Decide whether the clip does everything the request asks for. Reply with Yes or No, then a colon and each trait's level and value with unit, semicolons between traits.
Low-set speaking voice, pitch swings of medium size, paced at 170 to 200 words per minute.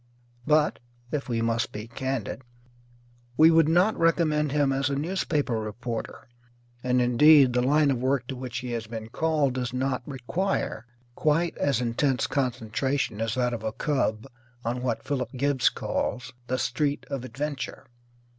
No: low, 130 Hz; average, 3.5 semitones; average, 155 wpm